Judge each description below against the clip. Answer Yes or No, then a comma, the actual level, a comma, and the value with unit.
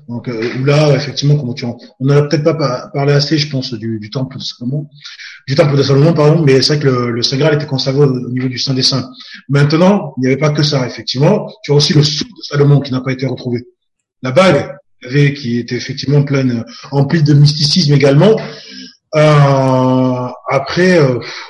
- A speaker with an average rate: Yes, average, 210 wpm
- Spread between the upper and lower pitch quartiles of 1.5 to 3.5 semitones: Yes, narrow, 2.6 semitones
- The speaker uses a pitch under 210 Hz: Yes, medium, 140 Hz